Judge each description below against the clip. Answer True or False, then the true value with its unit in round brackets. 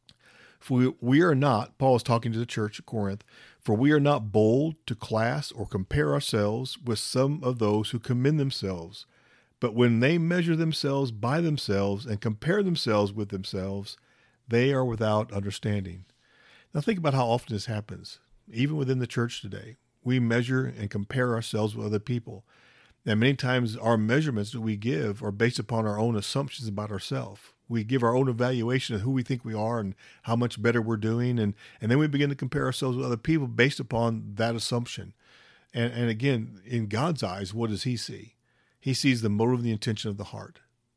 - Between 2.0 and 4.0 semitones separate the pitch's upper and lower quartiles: True (3.3 semitones)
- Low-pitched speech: True (120 Hz)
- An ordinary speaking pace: True (195 wpm)